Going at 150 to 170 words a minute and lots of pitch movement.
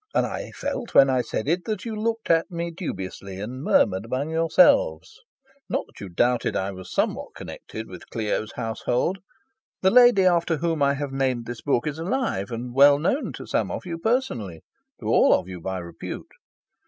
No: average, 190 wpm; wide, 8.0 semitones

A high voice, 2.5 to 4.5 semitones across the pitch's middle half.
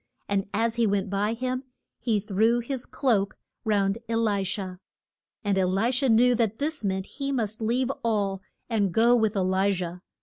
Yes: high, 220 Hz; average, 3.3 semitones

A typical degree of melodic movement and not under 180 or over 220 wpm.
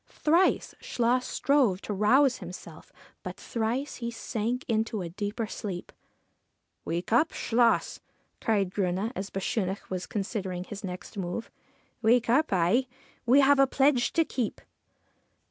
No: average, 4.6 semitones; average, 150 wpm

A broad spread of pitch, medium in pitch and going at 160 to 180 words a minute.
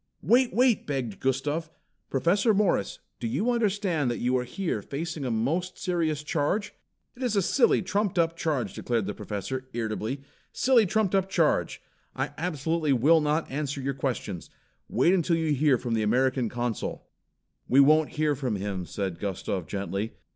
Yes: wide, 6.5 semitones; medium, 145 Hz; average, 165 wpm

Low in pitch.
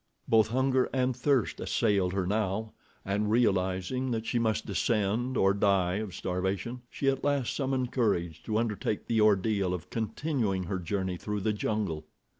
Yes: low, 105 Hz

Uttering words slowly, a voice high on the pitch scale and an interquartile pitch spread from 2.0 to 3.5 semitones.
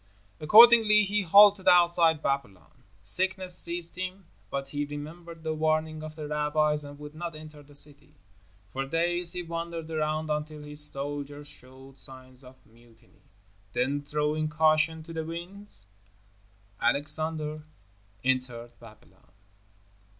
No: slow, 130 wpm; medium, 155 Hz; average, 2.8 semitones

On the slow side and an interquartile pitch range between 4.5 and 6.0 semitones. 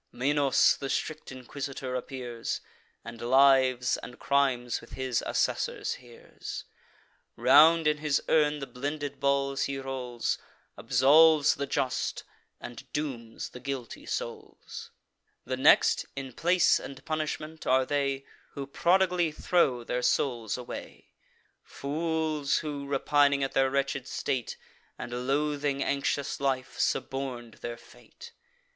No: slow, 120 wpm; narrow, 2.5 semitones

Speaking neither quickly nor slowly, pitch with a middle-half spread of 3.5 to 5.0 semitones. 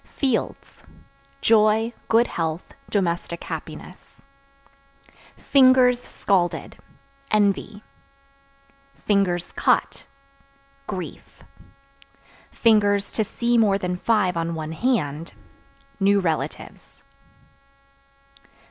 No: slow, 65 wpm; average, 4.6 semitones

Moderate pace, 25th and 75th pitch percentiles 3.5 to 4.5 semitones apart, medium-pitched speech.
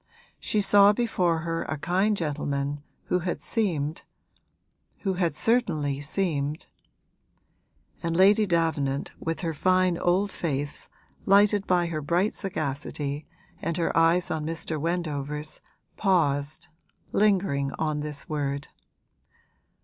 No: slow, 120 wpm; average, 4.1 semitones; medium, 165 Hz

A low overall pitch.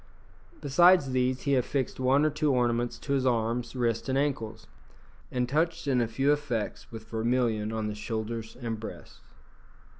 Yes: low, 125 Hz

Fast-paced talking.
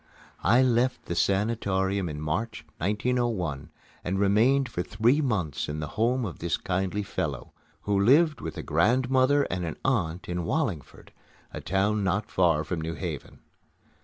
No: average, 155 wpm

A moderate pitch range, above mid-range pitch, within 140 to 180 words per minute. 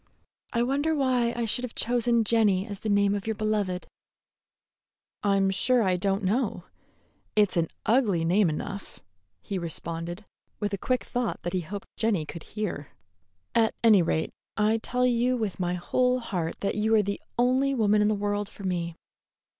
Yes: average, 3.9 semitones; high, 210 Hz; average, 175 wpm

